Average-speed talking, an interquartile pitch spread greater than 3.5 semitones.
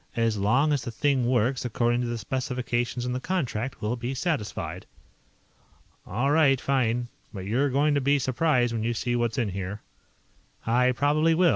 No: average, 175 wpm; average, 3.0 semitones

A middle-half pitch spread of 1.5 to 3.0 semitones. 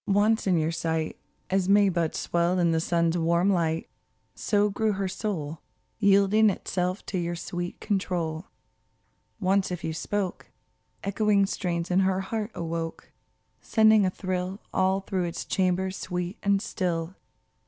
Yes: narrow, 2.6 semitones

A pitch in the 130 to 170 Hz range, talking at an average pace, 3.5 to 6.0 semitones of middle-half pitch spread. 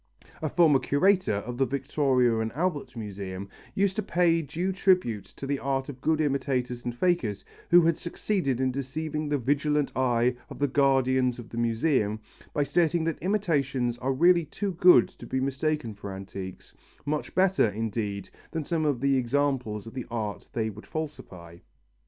Yes: low, 135 Hz; average, 170 wpm; average, 5.0 semitones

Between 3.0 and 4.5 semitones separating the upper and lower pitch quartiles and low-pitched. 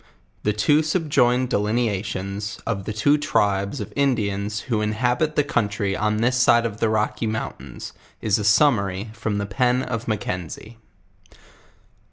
Yes: average, 3.3 semitones; low, 110 Hz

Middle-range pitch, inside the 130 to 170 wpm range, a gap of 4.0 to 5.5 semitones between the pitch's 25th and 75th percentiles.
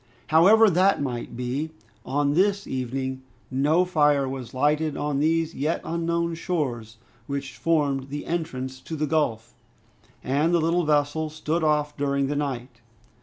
No: medium, 150 Hz; average, 145 wpm; average, 3.5 semitones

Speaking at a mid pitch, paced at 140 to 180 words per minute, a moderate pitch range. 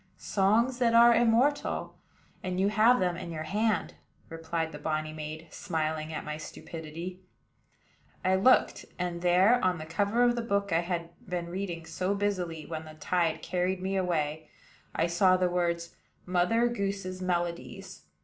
Yes: medium, 180 Hz; average, 160 wpm; average, 3.6 semitones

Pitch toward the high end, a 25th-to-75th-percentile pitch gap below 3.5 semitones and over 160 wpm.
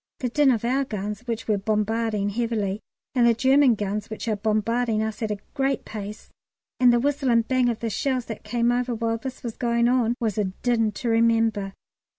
Yes: high, 230 Hz; narrow, 2.4 semitones; fast, 205 wpm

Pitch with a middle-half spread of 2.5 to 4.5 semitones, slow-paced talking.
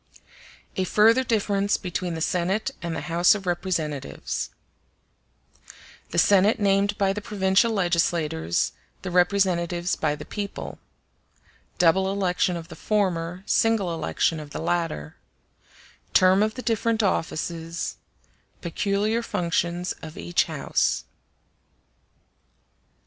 Yes: average, 3.1 semitones; slow, 105 wpm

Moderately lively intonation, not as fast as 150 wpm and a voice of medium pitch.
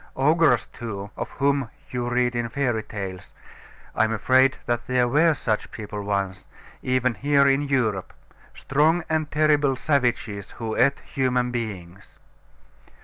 No: average, 4.2 semitones; average, 140 wpm; low, 125 Hz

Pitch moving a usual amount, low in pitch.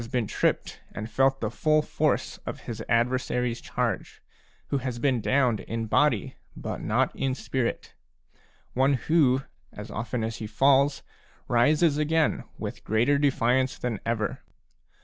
Yes: average, 3.3 semitones; low, 130 Hz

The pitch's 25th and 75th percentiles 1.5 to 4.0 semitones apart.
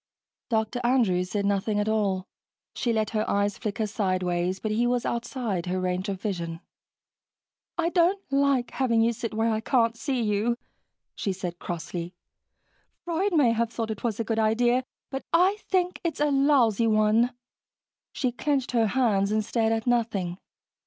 Yes: average, 3.5 semitones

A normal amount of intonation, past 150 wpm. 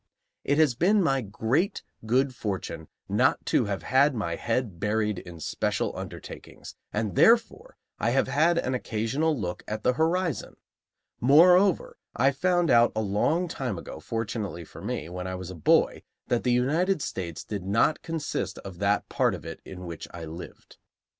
No: wide, 8.1 semitones; average, 170 wpm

